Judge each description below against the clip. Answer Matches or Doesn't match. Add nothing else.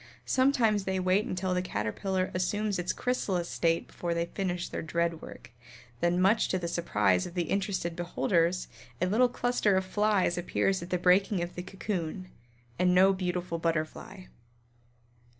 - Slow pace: Doesn't match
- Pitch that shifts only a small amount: Matches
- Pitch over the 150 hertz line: Matches